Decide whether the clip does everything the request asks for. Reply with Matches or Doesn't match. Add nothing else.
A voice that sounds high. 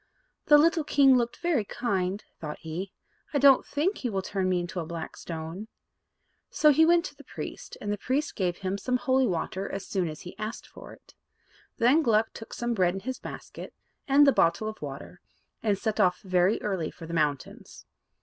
Matches